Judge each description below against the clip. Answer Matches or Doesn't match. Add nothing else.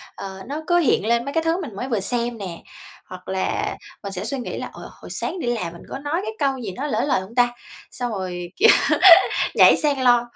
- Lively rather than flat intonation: Matches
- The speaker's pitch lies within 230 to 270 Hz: Matches